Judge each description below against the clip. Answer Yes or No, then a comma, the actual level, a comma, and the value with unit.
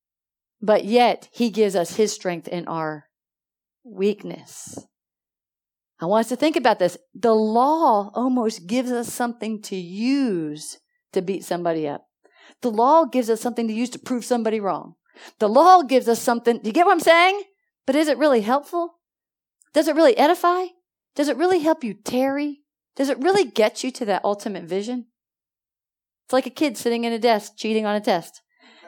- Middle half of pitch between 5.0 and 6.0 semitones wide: Yes, wide, 5.4 semitones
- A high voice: Yes, high, 240 Hz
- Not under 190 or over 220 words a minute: No, average, 180 wpm